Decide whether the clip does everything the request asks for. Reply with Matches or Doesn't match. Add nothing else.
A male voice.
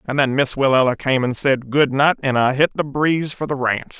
Matches